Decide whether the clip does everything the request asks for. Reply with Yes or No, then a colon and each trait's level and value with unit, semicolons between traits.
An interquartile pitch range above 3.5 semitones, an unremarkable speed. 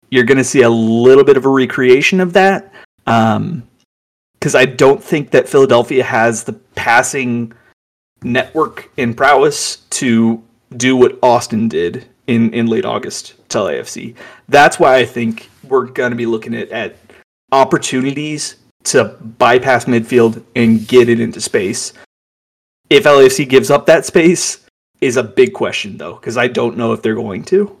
Yes: average, 4.2 semitones; average, 160 wpm